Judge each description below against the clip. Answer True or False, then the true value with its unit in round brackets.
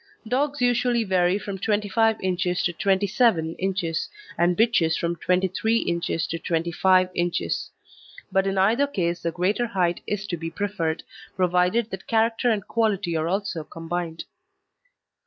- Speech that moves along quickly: False (140 wpm)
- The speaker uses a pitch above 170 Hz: True (190 Hz)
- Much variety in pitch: False (4.0 semitones)